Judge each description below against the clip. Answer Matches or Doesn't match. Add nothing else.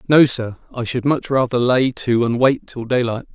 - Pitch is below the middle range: Matches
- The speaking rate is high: Matches